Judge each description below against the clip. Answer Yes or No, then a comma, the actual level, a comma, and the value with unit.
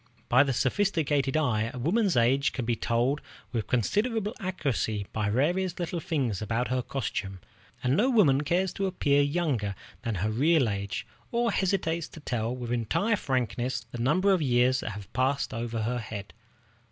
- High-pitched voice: No, low, 130 Hz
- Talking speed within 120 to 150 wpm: No, average, 175 wpm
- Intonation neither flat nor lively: No, wide, 6.6 semitones